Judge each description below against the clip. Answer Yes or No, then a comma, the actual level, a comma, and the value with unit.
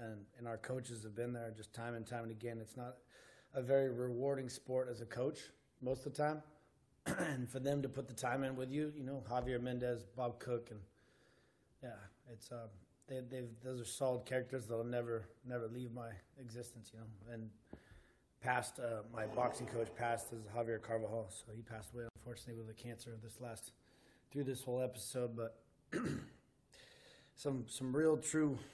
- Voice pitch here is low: Yes, low, 120 Hz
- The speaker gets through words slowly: No, average, 190 wpm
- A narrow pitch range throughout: Yes, narrow, 2.1 semitones